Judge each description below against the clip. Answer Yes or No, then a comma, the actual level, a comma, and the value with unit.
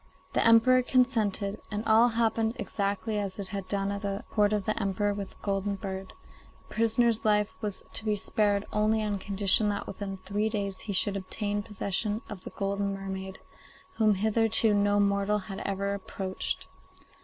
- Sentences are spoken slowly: No, average, 175 wpm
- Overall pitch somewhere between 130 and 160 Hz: No, high, 205 Hz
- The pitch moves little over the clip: Yes, narrow, 1.6 semitones